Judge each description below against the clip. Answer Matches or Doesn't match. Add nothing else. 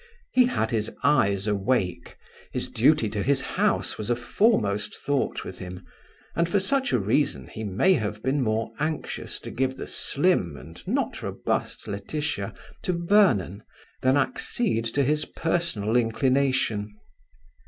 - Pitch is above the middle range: Doesn't match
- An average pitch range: Doesn't match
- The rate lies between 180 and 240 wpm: Doesn't match